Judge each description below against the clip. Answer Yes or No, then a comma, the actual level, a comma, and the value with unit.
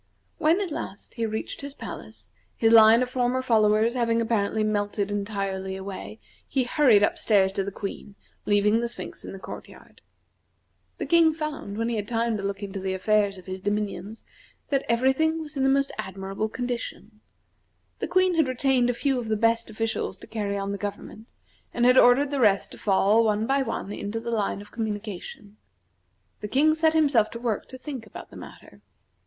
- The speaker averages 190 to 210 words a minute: Yes, average, 195 wpm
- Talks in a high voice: Yes, high, 225 Hz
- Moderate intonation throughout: Yes, average, 4.0 semitones